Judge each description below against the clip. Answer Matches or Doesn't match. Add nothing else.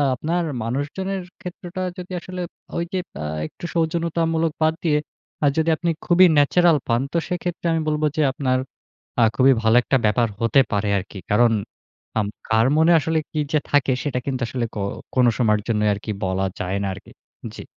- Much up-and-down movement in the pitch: Matches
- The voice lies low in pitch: Doesn't match